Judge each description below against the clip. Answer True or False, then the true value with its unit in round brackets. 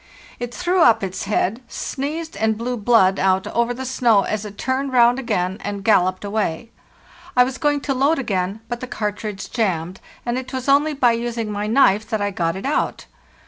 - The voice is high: True (230 Hz)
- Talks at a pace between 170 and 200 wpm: True (195 wpm)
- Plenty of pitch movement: False (4.3 semitones)